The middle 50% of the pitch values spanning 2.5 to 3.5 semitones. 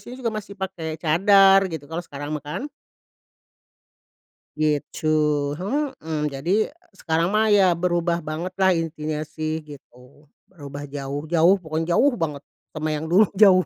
No: average, 3.9 semitones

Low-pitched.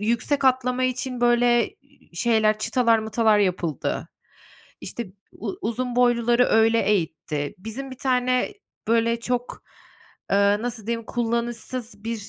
No: high, 235 Hz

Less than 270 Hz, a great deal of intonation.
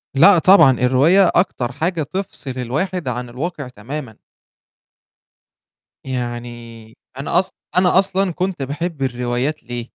Yes: low, 135 Hz; wide, 6.4 semitones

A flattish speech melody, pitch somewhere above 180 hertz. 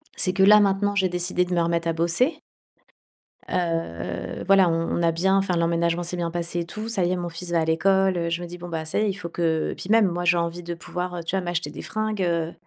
No: narrow, 2.3 semitones; medium, 175 Hz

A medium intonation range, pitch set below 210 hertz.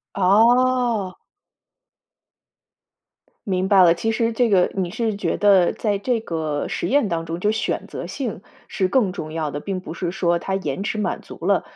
Yes: average, 4.2 semitones; high, 195 Hz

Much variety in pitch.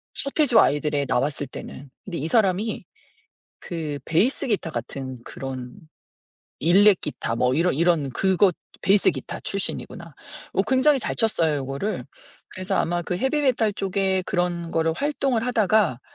Yes: wide, 6.6 semitones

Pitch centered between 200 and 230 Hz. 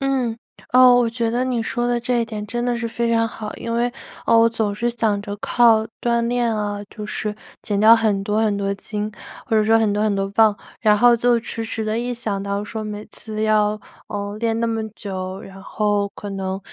Yes: high, 220 Hz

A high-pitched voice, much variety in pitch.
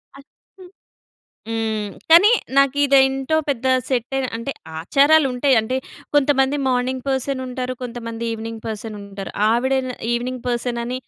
No: very high, 255 Hz; average, 2.7 semitones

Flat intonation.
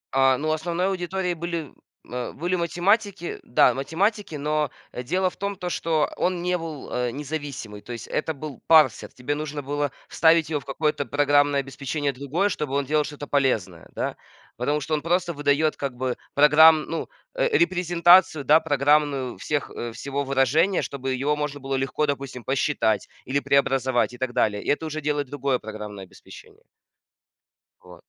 No: average, 3.3 semitones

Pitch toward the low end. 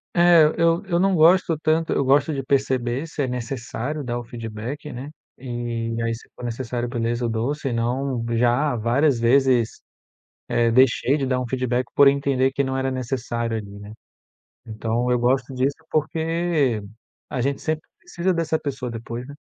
Yes: low, 130 Hz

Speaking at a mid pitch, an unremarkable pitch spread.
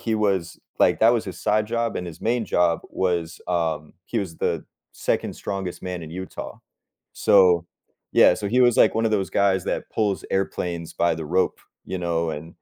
No: very low, 95 Hz; average, 3.9 semitones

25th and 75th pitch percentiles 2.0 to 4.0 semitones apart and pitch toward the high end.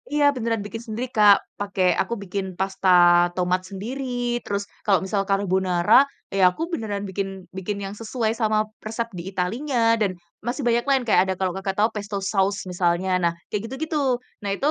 Yes: average, 3.1 semitones; high, 205 Hz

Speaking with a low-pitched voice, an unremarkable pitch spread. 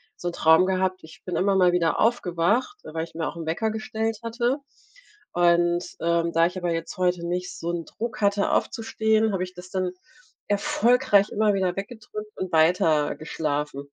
No: medium, 185 Hz; average, 4.0 semitones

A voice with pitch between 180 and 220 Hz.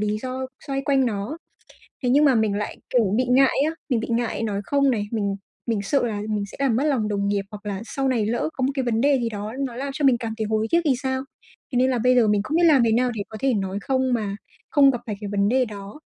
No: high, 235 Hz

